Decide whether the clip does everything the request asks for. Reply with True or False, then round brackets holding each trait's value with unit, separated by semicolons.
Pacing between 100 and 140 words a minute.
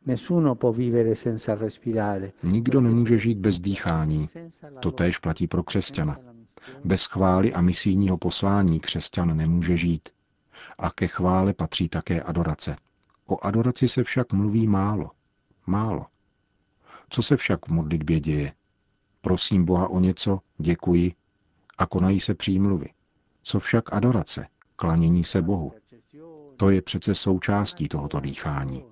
True (120 wpm)